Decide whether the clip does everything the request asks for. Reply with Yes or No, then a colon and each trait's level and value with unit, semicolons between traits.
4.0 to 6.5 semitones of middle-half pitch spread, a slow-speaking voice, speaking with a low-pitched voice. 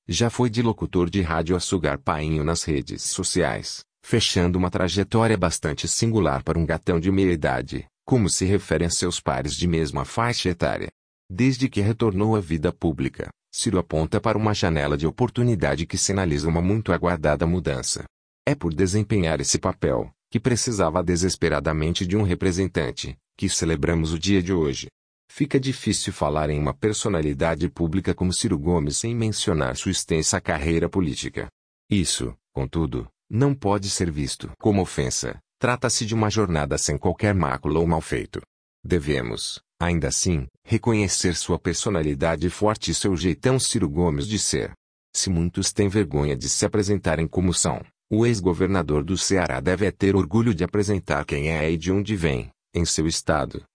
No: average, 4.4 semitones; average, 160 wpm; very low, 90 Hz